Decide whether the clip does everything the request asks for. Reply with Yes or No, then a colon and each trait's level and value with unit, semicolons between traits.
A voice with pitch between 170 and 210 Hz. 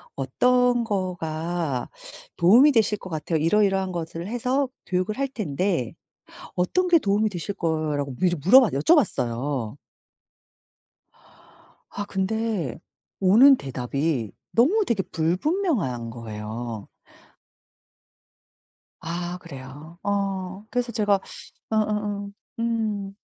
Yes: medium, 185 Hz